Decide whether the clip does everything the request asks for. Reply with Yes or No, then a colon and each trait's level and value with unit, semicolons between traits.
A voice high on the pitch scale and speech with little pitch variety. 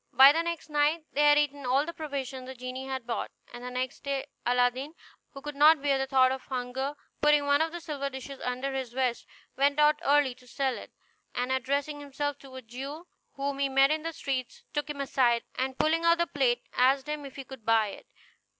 Yes: very high, 275 Hz; narrow, 2.3 semitones